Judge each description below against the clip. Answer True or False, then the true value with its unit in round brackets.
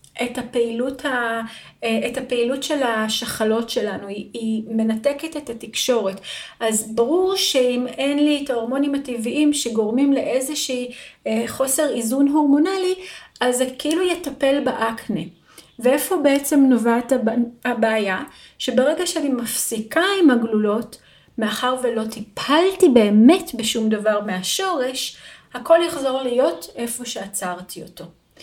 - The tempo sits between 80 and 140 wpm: True (110 wpm)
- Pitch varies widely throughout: False (4.0 semitones)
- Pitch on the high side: True (250 Hz)